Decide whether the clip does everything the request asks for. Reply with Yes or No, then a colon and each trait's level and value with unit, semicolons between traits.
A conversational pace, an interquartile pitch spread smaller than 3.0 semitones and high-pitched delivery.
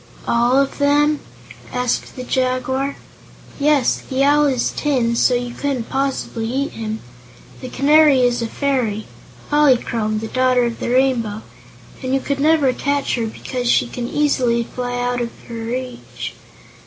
Yes: average, 155 wpm; narrow, 2.6 semitones; very high, 255 Hz